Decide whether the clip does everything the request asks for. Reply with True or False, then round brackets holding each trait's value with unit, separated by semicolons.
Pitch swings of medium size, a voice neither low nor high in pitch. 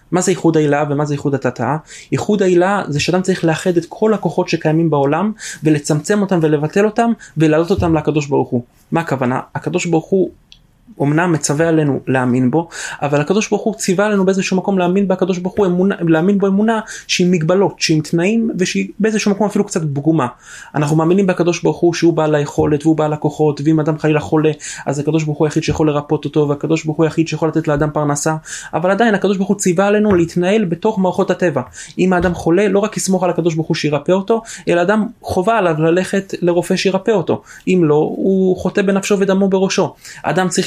True (3.9 semitones; 175 Hz)